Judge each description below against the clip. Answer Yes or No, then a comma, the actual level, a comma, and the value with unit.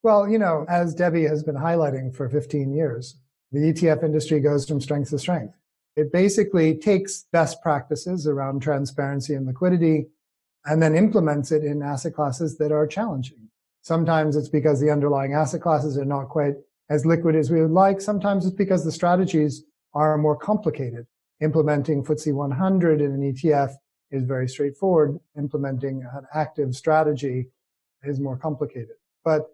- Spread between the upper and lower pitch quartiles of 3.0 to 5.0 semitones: No, narrow, 2.5 semitones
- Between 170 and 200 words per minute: No, average, 160 wpm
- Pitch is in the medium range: Yes, medium, 150 Hz